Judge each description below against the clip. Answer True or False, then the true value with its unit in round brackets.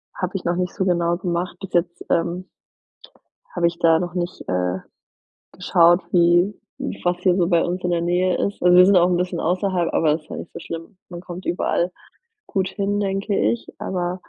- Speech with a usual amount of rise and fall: False (1.3 semitones)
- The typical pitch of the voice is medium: True (175 Hz)